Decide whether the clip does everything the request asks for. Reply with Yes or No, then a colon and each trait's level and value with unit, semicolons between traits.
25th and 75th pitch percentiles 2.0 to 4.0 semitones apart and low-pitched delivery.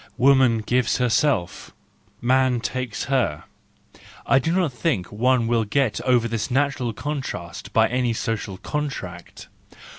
Yes: average, 3.2 semitones; low, 125 Hz